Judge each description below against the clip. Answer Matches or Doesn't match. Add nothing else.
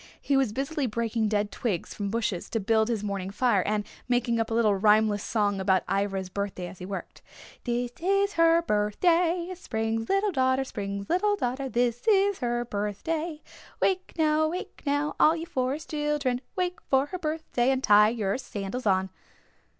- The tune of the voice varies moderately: Doesn't match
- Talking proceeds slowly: Doesn't match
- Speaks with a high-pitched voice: Matches